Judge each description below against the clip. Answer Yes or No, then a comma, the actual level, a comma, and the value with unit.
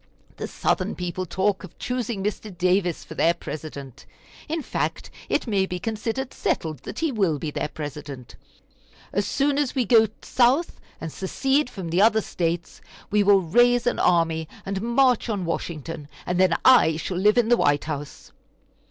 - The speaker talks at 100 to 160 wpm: No, average, 170 wpm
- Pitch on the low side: No, high, 190 Hz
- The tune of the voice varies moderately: No, wide, 6.3 semitones